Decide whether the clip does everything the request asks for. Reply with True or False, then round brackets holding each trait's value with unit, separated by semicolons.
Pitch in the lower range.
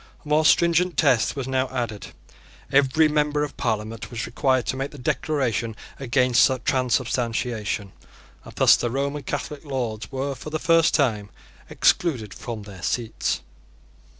True (130 Hz)